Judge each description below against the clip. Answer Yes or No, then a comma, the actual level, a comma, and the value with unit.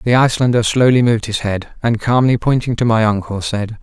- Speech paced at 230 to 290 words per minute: No, fast, 205 wpm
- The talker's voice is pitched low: Yes, low, 115 Hz